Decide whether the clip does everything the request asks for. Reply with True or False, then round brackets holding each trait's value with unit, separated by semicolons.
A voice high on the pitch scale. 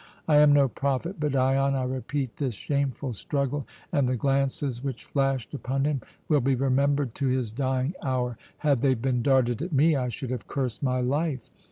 False (135 Hz)